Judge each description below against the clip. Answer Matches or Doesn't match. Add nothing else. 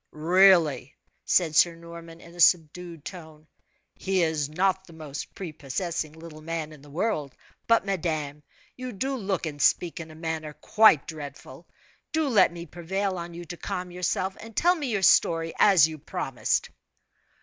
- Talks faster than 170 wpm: Doesn't match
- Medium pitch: Matches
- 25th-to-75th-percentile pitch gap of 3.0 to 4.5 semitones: Matches